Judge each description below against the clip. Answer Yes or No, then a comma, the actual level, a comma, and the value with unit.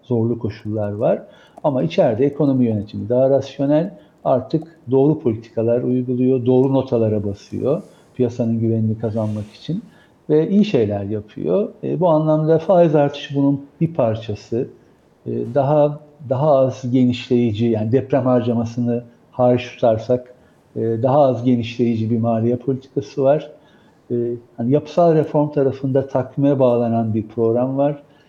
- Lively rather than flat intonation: No, average, 3.6 semitones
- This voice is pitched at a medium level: No, low, 125 Hz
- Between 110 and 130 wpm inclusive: Yes, average, 125 wpm